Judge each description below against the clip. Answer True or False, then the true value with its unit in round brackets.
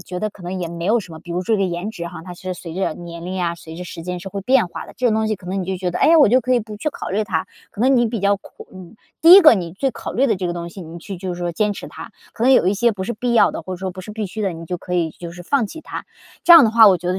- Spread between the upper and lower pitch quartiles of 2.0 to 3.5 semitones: False (3.9 semitones)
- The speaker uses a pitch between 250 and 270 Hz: False (190 Hz)